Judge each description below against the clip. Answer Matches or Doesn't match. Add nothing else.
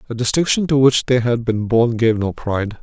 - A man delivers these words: Matches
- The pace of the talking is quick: Matches